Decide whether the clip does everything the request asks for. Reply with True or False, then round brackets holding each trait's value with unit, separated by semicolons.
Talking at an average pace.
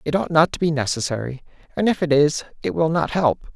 False (235 wpm)